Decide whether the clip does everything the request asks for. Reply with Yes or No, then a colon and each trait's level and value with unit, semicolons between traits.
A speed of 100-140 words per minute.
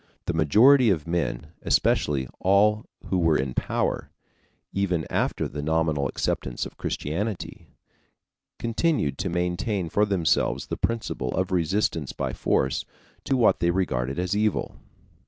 Yes: slow, 135 wpm